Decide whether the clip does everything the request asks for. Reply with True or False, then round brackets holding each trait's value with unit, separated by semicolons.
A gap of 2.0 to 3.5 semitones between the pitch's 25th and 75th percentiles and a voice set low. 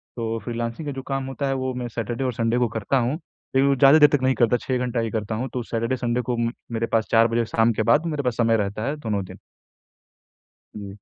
True (2.5 semitones; 120 Hz)